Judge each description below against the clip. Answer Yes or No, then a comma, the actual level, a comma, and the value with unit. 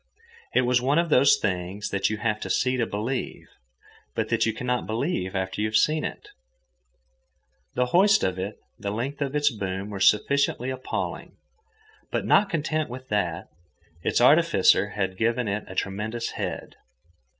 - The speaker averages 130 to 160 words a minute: No, average, 175 wpm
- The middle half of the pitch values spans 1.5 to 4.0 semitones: No, average, 4.8 semitones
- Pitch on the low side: Yes, low, 115 Hz